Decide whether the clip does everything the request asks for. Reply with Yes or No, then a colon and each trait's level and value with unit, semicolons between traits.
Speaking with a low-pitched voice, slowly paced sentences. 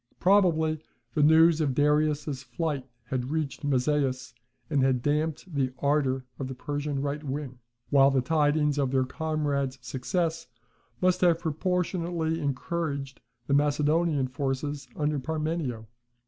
No: medium, 145 Hz; slow, 130 wpm